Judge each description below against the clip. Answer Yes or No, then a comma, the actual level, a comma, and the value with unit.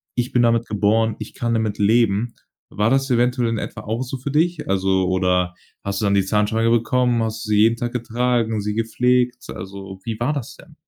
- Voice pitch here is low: Yes, low, 115 Hz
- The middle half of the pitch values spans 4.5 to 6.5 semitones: No, average, 2.9 semitones